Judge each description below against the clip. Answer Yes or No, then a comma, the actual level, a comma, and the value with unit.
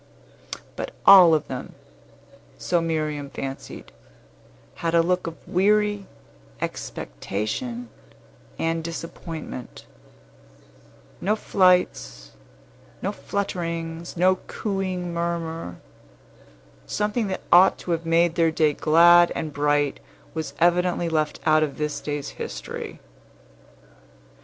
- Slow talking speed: Yes, slow, 100 wpm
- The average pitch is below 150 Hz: No, medium, 165 Hz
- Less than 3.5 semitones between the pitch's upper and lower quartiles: Yes, average, 2.7 semitones